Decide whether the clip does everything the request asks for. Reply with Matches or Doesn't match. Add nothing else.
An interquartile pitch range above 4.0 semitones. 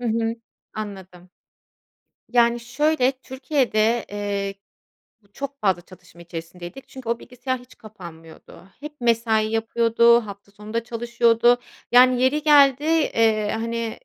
Doesn't match